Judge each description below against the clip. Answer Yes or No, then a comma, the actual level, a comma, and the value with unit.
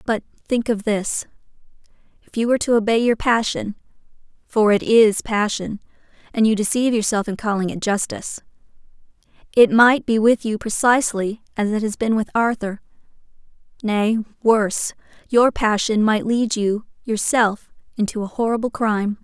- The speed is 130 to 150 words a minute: Yes, average, 140 wpm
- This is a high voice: Yes, high, 220 Hz